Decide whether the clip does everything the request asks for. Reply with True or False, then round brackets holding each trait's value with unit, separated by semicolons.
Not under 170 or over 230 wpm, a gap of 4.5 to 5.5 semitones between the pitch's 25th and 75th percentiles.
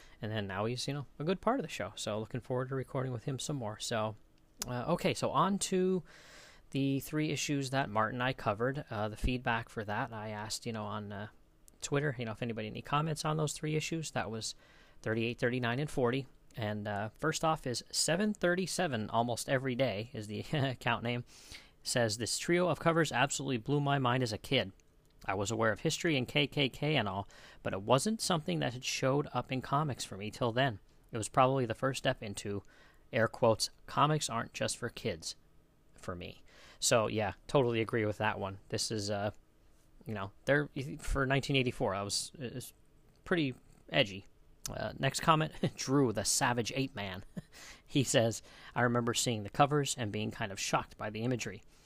True (200 wpm; 4.9 semitones)